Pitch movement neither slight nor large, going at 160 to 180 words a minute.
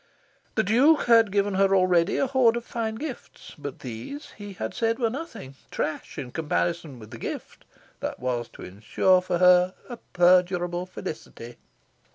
No: wide, 6.2 semitones; average, 165 wpm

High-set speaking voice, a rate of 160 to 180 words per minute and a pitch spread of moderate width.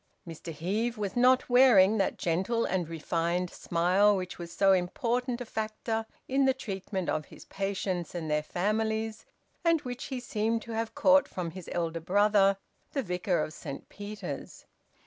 Yes: high, 200 Hz; average, 165 wpm; average, 4.5 semitones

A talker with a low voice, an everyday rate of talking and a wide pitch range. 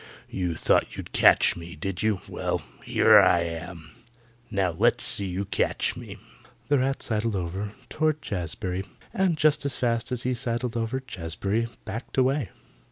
Yes: low, 105 Hz; average, 160 wpm; wide, 6.1 semitones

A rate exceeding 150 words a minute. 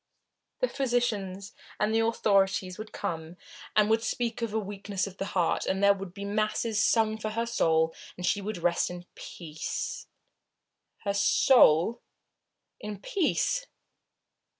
No: average, 145 wpm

